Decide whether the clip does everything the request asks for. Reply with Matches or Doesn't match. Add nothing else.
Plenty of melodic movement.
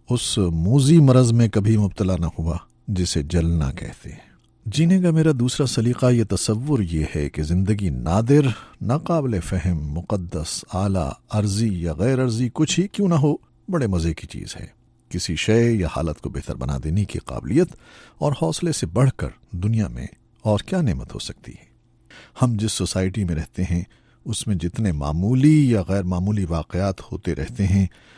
Matches